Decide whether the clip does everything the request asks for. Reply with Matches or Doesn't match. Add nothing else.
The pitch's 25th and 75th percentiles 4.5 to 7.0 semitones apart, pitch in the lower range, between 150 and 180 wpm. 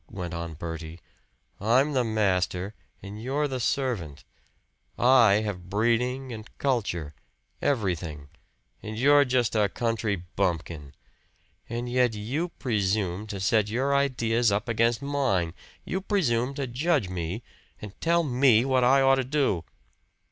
Doesn't match